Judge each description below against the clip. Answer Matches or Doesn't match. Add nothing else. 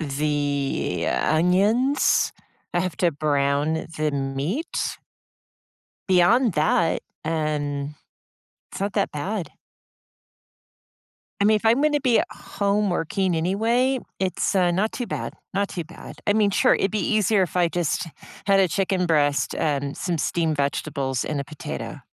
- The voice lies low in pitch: Doesn't match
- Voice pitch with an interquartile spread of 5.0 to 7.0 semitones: Matches